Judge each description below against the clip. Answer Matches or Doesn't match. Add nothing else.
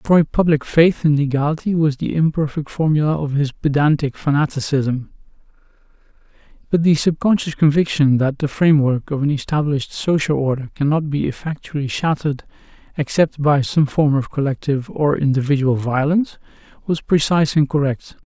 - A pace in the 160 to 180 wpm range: Doesn't match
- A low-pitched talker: Doesn't match